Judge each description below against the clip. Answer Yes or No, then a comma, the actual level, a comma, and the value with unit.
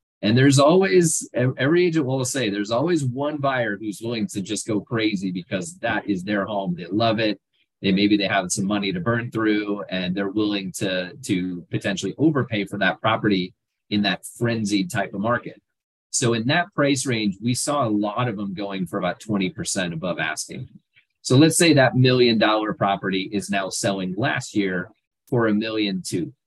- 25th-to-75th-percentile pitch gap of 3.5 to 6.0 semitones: Yes, average, 3.9 semitones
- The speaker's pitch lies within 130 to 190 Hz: No, low, 105 Hz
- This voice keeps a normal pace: Yes, average, 190 wpm